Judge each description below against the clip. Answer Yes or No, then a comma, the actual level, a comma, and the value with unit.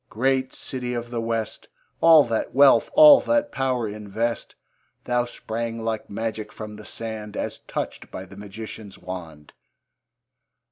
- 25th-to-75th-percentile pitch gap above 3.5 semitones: No, average, 2.9 semitones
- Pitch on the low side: Yes, low, 115 Hz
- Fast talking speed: No, average, 140 wpm